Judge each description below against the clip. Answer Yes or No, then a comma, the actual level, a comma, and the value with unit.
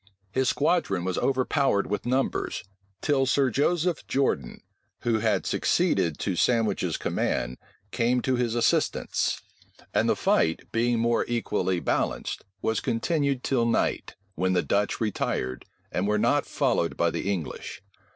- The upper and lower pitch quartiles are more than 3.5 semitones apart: Yes, average, 5.1 semitones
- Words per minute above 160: No, average, 140 wpm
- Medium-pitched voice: No, low, 115 Hz